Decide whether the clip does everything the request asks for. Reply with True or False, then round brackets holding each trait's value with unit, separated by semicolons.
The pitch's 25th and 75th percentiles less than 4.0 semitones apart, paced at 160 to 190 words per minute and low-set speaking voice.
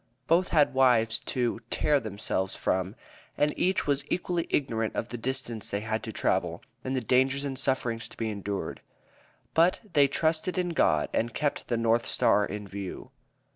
False (4.7 semitones; 175 wpm; 125 Hz)